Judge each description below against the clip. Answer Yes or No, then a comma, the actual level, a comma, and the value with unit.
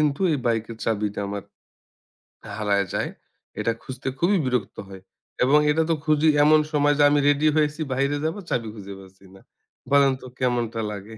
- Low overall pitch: Yes, low, 130 Hz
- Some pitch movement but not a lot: No, wide, 5.7 semitones